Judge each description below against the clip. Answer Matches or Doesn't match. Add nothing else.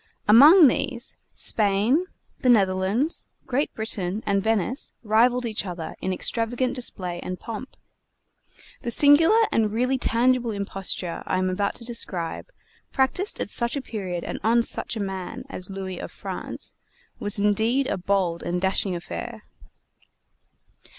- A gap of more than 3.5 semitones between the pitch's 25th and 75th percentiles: Matches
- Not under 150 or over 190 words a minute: Doesn't match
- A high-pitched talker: Matches